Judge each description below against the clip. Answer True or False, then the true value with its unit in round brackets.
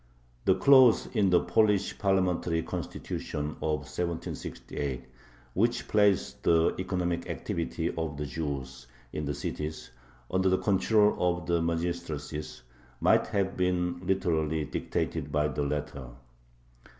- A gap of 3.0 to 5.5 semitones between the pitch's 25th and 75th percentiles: True (3.8 semitones)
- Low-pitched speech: True (85 Hz)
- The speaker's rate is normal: False (120 wpm)